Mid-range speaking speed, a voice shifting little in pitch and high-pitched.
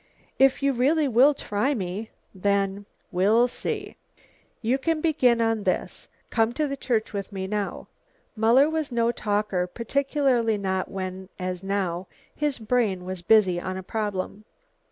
No: average, 155 wpm; average, 4.9 semitones; high, 220 Hz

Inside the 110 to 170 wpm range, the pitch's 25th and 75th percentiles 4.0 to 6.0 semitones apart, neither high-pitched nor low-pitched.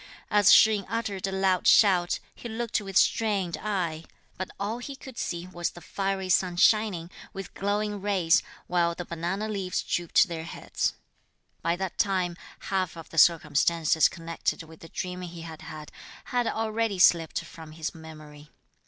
No: average, 165 wpm; average, 3.4 semitones; medium, 180 Hz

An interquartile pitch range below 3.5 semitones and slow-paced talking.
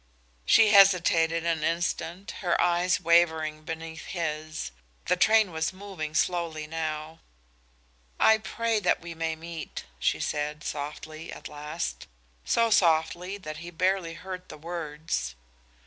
Yes: narrow, 2.5 semitones; slow, 130 wpm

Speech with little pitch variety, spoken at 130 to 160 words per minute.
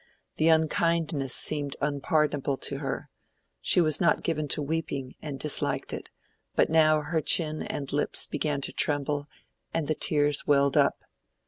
Yes: narrow, 1.9 semitones; average, 150 wpm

